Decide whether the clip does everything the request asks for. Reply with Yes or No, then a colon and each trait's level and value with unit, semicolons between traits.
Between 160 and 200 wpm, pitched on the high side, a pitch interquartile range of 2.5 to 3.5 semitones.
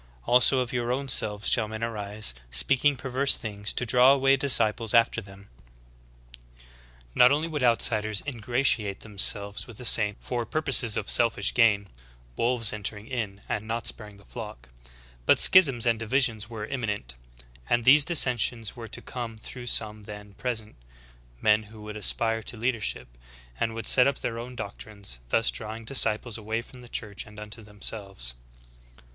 No: average, 170 wpm; low, 110 Hz; average, 2.9 semitones